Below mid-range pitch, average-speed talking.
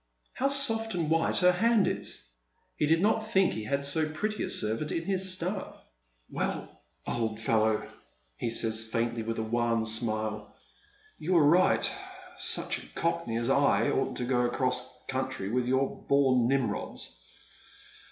Yes: low, 130 Hz; average, 165 wpm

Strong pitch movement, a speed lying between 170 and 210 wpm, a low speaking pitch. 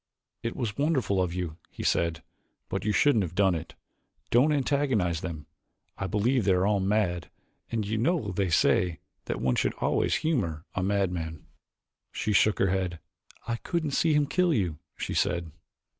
Yes: wide, 5.7 semitones; average, 175 wpm; low, 100 Hz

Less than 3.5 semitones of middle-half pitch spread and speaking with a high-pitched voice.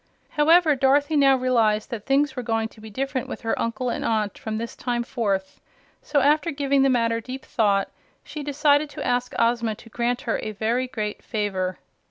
No: average, 3.8 semitones; high, 245 Hz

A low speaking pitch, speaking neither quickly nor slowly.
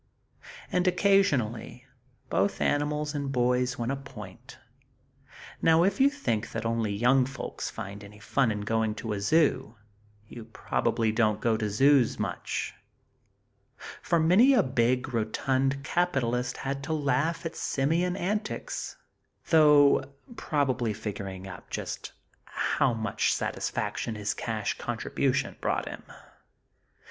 No: low, 125 Hz; slow, 125 wpm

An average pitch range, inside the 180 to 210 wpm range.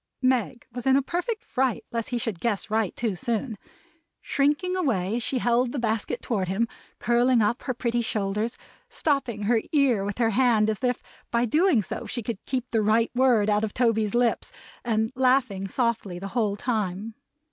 Yes: average, 3.0 semitones; average, 185 wpm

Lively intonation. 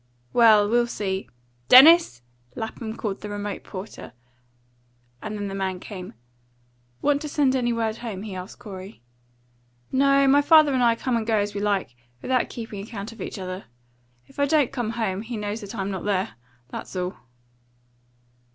No: average, 3.7 semitones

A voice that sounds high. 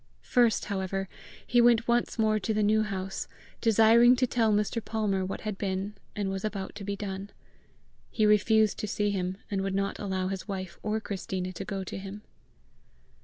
Yes: high, 205 Hz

